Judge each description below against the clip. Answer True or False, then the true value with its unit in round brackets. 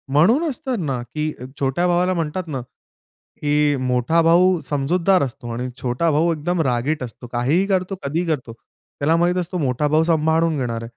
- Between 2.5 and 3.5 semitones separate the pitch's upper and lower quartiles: False (5.1 semitones)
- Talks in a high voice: False (155 Hz)